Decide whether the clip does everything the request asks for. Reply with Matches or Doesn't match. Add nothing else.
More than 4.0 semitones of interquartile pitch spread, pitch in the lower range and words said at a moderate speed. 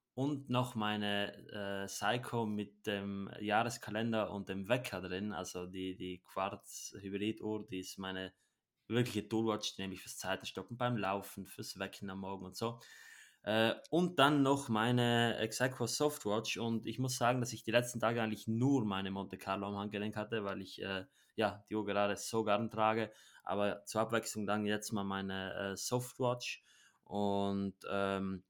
Doesn't match